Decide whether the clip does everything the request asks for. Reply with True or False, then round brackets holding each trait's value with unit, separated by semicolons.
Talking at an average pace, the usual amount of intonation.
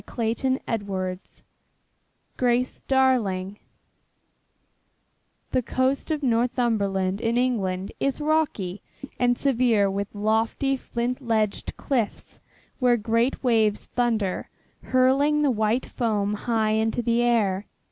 False (105 wpm; 3.5 semitones)